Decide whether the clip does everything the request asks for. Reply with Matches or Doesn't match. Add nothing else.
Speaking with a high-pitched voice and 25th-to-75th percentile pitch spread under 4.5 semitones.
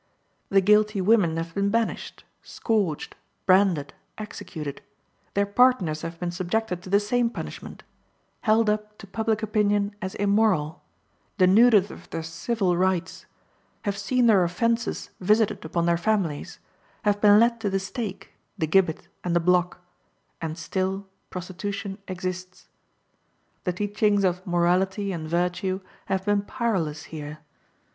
Matches